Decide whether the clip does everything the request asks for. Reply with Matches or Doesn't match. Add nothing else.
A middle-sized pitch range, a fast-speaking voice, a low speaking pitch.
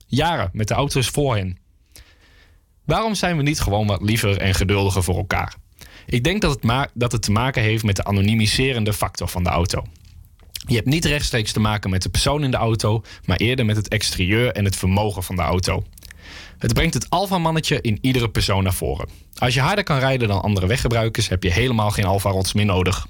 Matches